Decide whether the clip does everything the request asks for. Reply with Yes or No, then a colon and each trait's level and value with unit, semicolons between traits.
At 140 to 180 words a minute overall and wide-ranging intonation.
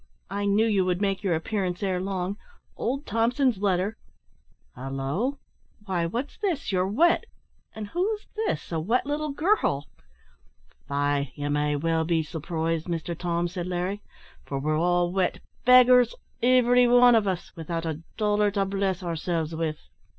Yes: average, 150 wpm; wide, 5.8 semitones